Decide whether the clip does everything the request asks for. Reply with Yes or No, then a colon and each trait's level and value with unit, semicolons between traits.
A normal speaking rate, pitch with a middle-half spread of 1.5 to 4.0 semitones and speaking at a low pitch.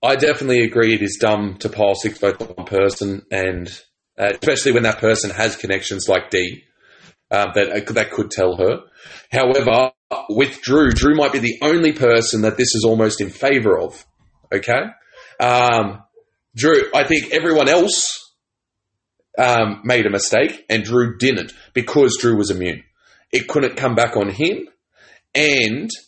Yes: average, 165 wpm; average, 3.7 semitones; low, 110 Hz